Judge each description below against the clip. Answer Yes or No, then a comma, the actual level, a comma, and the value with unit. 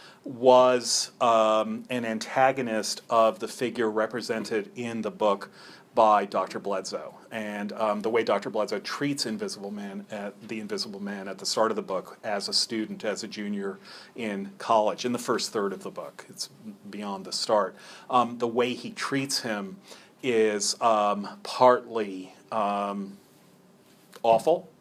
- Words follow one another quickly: No, average, 150 wpm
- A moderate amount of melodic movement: Yes, average, 3.4 semitones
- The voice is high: No, low, 110 Hz